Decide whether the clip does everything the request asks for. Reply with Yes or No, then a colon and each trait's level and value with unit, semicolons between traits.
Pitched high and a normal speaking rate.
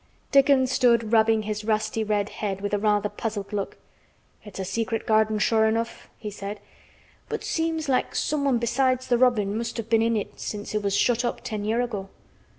Yes: high, 220 Hz; average, 190 wpm